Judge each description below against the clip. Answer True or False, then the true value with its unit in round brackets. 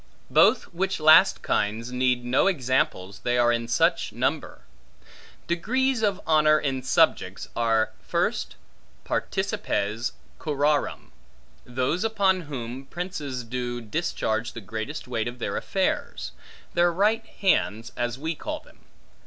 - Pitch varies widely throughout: True (6.3 semitones)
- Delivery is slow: True (125 wpm)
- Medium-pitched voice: False (130 Hz)